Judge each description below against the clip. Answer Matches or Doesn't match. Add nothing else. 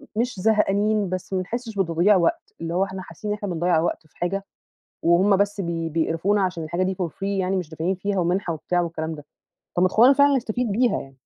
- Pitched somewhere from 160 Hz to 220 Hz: Matches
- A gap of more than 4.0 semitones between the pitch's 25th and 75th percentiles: Doesn't match